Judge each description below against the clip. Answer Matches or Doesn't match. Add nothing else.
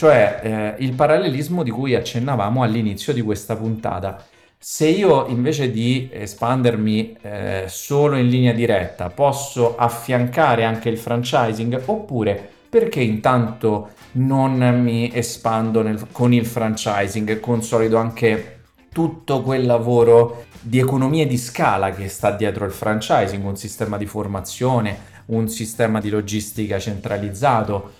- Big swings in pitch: Doesn't match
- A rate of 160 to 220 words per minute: Doesn't match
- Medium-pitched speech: Doesn't match